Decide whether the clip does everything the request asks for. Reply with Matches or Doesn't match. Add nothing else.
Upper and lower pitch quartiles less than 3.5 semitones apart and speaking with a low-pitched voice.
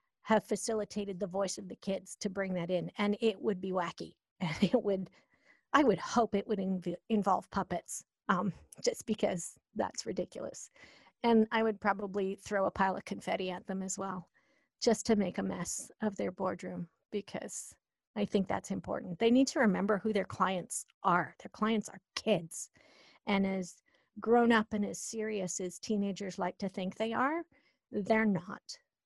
Doesn't match